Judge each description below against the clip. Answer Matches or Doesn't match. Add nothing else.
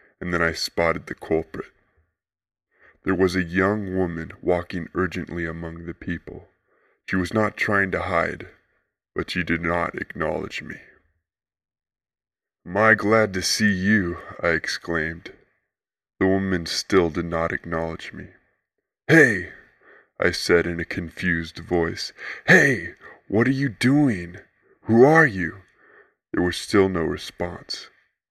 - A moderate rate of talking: Doesn't match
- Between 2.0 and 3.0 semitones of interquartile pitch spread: Matches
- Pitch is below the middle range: Matches